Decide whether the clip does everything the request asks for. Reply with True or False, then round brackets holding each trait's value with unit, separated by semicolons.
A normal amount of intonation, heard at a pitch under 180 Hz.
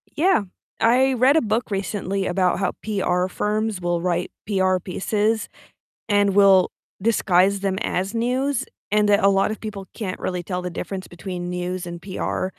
False (3.0 semitones; 195 Hz)